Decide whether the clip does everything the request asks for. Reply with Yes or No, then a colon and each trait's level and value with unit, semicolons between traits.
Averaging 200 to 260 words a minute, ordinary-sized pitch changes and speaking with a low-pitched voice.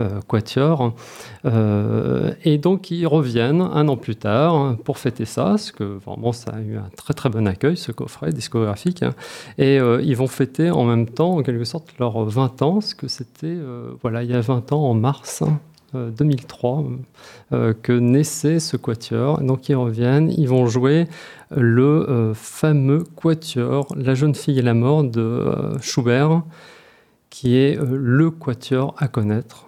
No: average, 175 wpm; average, 4.1 semitones; low, 130 Hz